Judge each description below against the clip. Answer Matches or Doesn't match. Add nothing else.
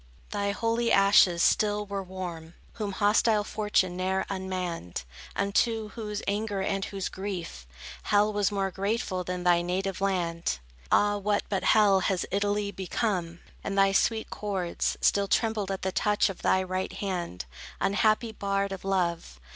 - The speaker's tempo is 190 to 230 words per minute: Doesn't match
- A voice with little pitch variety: Matches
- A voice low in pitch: Doesn't match